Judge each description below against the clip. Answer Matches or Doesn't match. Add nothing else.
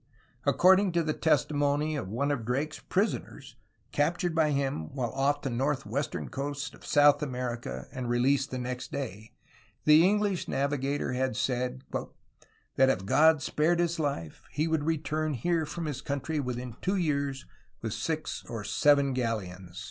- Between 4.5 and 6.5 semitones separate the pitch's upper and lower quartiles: Doesn't match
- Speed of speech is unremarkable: Matches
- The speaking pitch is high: Doesn't match